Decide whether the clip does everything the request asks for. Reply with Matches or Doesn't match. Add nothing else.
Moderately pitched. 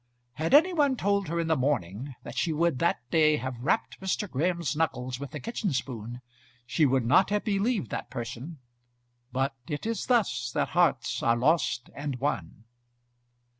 Matches